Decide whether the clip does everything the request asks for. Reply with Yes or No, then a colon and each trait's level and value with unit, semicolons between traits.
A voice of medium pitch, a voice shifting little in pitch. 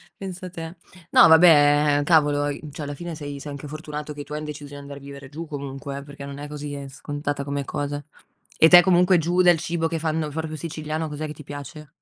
Yes: medium, 150 Hz; narrow, 2.0 semitones